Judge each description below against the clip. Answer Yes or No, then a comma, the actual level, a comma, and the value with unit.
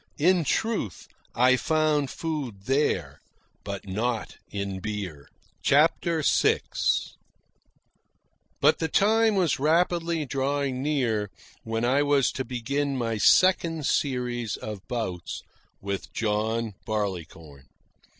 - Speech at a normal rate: No, slow, 105 wpm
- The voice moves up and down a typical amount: No, wide, 6.2 semitones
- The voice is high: No, low, 130 Hz